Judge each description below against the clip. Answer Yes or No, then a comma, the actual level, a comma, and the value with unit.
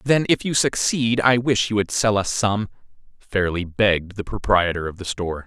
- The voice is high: No, low, 105 Hz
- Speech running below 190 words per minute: No, average, 200 wpm